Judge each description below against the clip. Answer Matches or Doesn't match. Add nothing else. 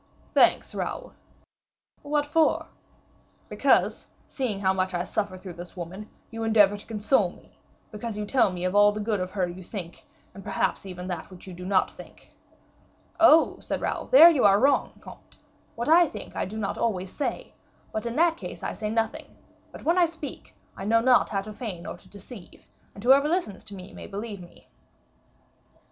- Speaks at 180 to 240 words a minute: Matches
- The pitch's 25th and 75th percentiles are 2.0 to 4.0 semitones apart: Doesn't match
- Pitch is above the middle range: Matches